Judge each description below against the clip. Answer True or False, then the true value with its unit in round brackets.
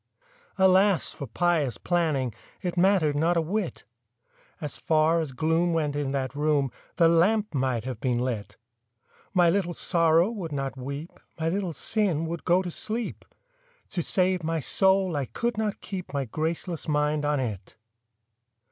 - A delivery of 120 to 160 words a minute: True (155 wpm)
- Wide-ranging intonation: False (4.1 semitones)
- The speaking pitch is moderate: True (165 Hz)